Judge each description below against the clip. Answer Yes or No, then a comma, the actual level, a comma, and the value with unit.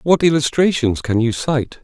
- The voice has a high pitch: No, low, 135 Hz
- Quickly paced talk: No, average, 165 wpm